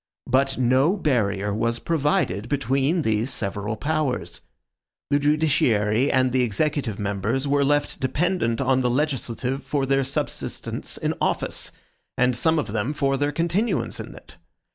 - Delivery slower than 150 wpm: Yes, average, 140 wpm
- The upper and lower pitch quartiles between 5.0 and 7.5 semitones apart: No, average, 4.1 semitones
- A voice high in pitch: No, low, 135 Hz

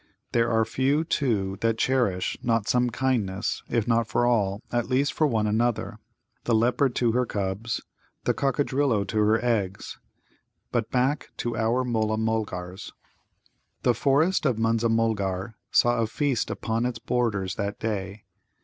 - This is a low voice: Yes, low, 115 Hz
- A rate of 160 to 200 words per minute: No, average, 150 wpm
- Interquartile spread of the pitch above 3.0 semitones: No, narrow, 2.5 semitones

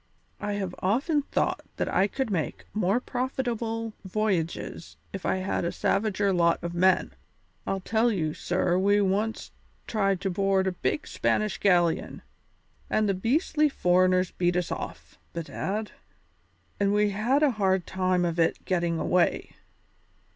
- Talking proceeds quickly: No, average, 145 wpm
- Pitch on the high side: Yes, high, 195 Hz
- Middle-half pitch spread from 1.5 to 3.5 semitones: Yes, average, 3.2 semitones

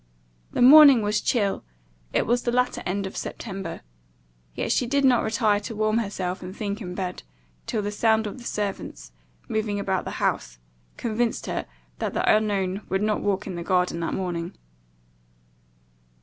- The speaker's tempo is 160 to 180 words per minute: Yes, average, 170 wpm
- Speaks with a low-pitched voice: No, high, 205 Hz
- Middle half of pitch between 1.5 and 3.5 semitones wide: Yes, average, 2.9 semitones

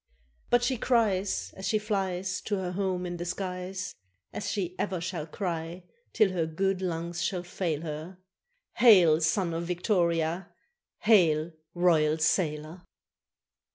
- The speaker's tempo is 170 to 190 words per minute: No, slow, 135 wpm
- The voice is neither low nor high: Yes, medium, 180 Hz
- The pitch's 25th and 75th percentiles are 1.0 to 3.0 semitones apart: Yes, narrow, 2.6 semitones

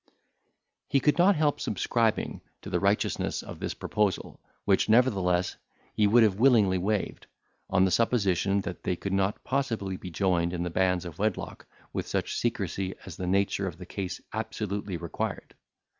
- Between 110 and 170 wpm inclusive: Yes, average, 165 wpm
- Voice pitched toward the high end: No, very low, 95 Hz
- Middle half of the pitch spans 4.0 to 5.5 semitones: No, average, 3.0 semitones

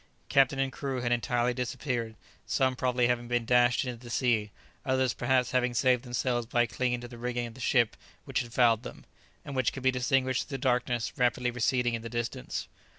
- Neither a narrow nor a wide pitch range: No, narrow, 1.3 semitones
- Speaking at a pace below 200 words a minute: No, fast, 205 wpm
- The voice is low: Yes, low, 125 Hz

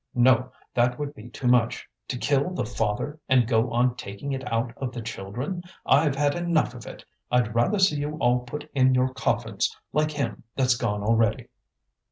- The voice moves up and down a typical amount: Yes, average, 3.5 semitones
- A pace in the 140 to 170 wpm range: No, average, 190 wpm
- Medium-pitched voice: No, low, 125 Hz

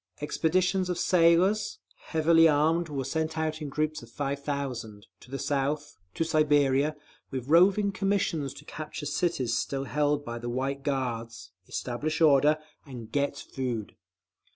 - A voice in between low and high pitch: Yes, medium, 145 Hz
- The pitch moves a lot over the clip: No, average, 3.2 semitones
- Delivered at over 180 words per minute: No, average, 145 wpm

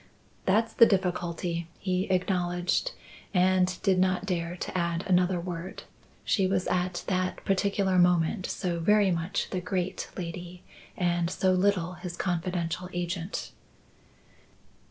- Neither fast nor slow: No, slow, 125 wpm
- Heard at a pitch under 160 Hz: No, medium, 180 Hz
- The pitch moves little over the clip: Yes, narrow, 1.3 semitones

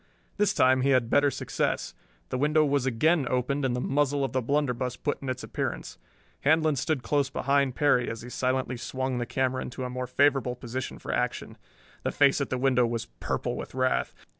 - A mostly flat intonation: Yes, narrow, 2.1 semitones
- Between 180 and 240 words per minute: Yes, average, 200 wpm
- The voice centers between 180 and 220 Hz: No, low, 130 Hz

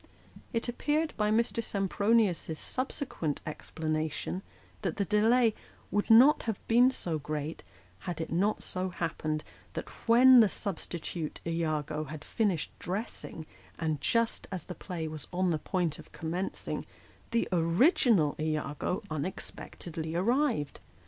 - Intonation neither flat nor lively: No, wide, 6.2 semitones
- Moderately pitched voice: Yes, medium, 180 Hz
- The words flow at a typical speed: No, slow, 130 wpm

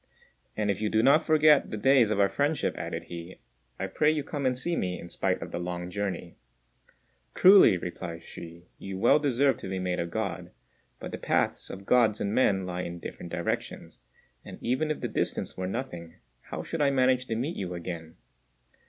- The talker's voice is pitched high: No, low, 105 Hz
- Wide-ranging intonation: Yes, wide, 7.2 semitones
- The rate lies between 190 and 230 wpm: Yes, average, 200 wpm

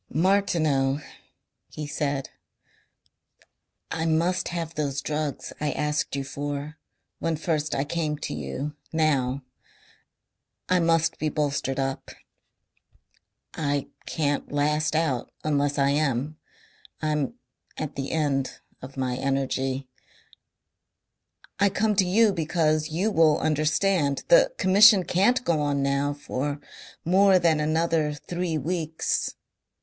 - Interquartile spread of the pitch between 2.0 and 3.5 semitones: Yes, average, 2.8 semitones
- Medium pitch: Yes, medium, 150 Hz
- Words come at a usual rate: No, slow, 115 wpm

